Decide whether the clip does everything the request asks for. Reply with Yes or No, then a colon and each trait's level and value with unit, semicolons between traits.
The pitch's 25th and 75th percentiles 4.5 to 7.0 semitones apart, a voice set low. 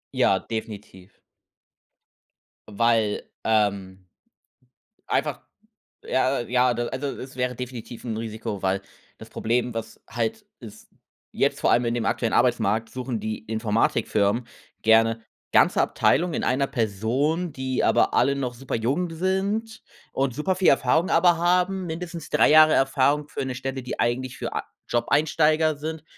Yes: average, 5.2 semitones; low, 125 Hz